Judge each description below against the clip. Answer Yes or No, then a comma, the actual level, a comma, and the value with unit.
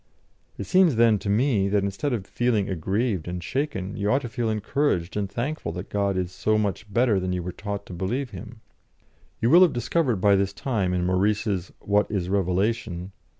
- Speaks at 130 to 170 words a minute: No, average, 195 wpm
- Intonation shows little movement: No, average, 4.0 semitones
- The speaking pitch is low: Yes, low, 100 Hz